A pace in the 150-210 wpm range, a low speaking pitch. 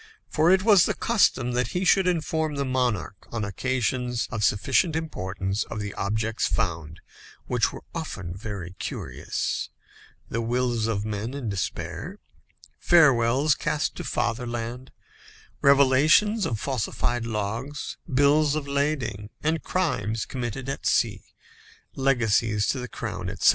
No: slow, 135 wpm; low, 125 Hz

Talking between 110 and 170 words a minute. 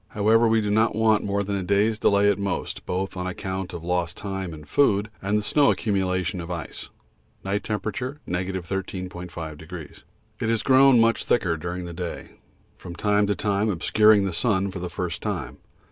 No: average, 180 wpm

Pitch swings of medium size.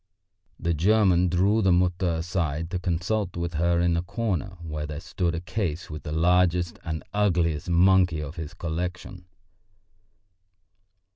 No: narrow, 1.8 semitones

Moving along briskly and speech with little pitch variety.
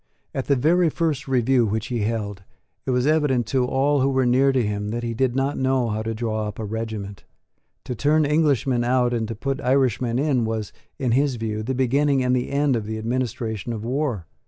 No: fast, 215 wpm; average, 3.3 semitones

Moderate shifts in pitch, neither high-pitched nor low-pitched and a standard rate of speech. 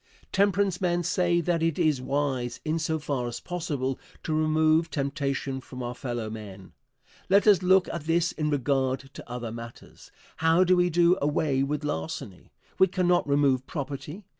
Yes: average, 4.7 semitones; medium, 150 Hz; average, 165 wpm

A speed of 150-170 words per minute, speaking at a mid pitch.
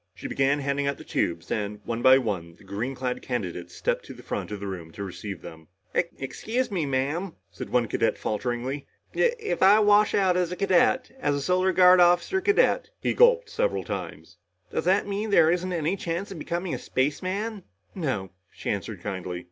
No: average, 195 wpm; medium, 150 Hz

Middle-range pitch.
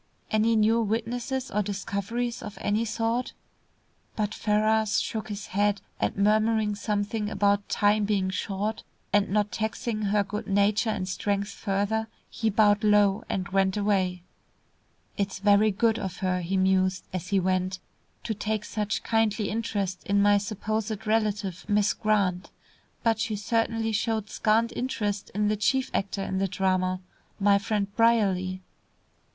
No: high, 210 Hz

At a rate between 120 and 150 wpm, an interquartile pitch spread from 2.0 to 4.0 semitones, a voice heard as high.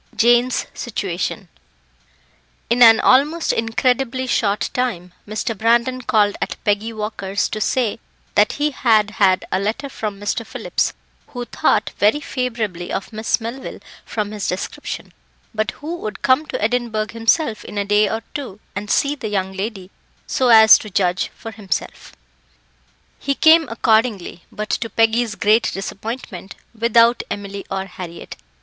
Yes: average, 145 wpm; average, 3.0 semitones; high, 220 Hz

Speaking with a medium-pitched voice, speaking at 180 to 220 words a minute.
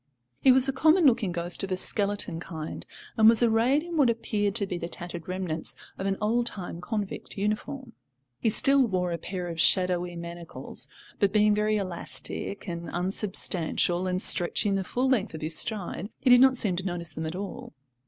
No: high, 195 Hz; average, 195 wpm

